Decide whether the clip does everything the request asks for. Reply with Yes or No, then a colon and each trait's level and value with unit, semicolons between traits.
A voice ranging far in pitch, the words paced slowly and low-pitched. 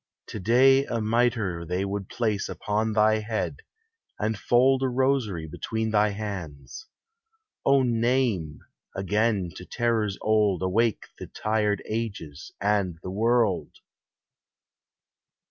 No: average, 3.3 semitones; slow, 115 wpm; low, 110 Hz